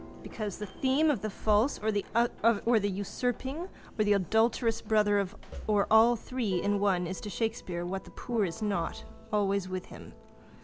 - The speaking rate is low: No, average, 165 wpm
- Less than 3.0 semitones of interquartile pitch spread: Yes, narrow, 2.5 semitones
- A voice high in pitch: Yes, high, 210 Hz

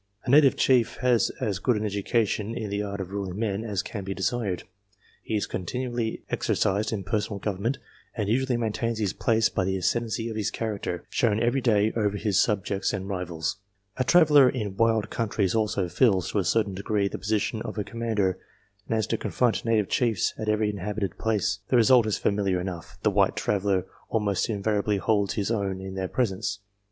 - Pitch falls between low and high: No, low, 105 Hz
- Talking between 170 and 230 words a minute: Yes, average, 195 wpm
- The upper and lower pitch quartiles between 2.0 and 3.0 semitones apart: Yes, narrow, 2.6 semitones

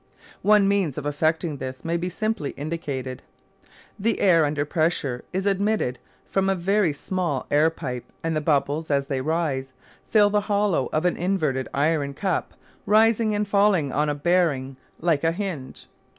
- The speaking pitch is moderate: Yes, medium, 165 Hz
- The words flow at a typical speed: Yes, average, 165 wpm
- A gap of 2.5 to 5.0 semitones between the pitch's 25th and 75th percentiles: No, wide, 5.4 semitones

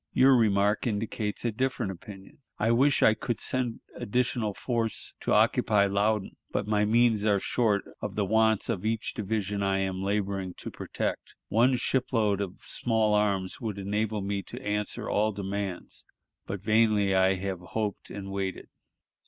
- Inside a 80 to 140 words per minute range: No, average, 160 wpm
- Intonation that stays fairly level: Yes, narrow, 2.2 semitones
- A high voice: No, low, 105 Hz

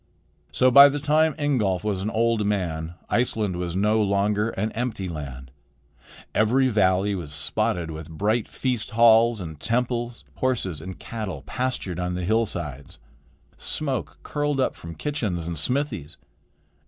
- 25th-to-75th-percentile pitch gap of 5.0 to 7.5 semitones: Yes, wide, 5.6 semitones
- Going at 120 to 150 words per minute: Yes, average, 140 wpm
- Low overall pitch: Yes, low, 105 Hz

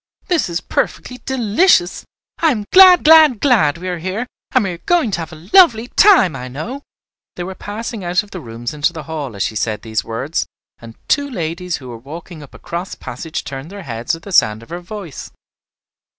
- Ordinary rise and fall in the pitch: No, wide, 7.8 semitones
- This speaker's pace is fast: Yes, fast, 210 wpm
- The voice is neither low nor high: Yes, medium, 175 Hz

